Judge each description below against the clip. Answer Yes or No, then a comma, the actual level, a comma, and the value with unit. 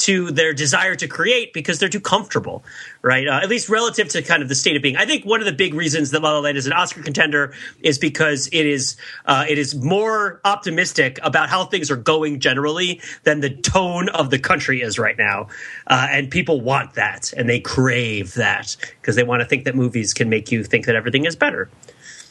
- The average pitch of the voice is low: No, medium, 150 Hz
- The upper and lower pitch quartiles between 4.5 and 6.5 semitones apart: Yes, average, 4.8 semitones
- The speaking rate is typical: No, fast, 225 wpm